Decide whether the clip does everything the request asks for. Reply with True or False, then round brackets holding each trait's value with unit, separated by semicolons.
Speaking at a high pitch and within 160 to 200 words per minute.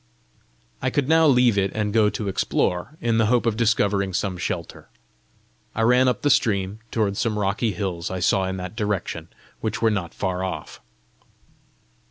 False (105 Hz; 175 wpm)